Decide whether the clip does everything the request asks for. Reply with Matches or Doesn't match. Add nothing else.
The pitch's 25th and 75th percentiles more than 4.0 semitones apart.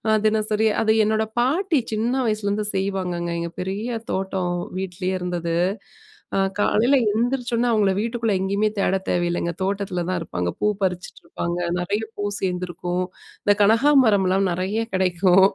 Doesn't match